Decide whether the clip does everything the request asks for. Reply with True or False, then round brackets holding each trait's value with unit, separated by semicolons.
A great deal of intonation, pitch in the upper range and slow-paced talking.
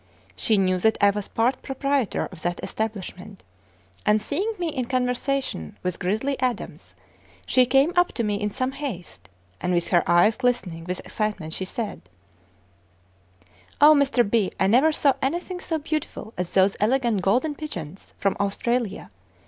False (5.9 semitones; 225 Hz; 155 wpm)